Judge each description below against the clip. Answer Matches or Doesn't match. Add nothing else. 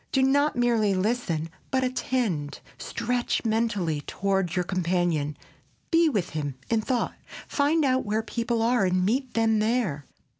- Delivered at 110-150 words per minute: Matches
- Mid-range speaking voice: Doesn't match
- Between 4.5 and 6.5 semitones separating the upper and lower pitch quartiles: Matches